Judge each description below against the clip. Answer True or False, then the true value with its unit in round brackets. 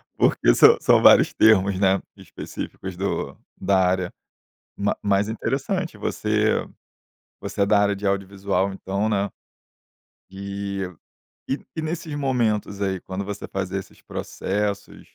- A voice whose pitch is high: False (100 Hz)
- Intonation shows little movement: True (1.7 semitones)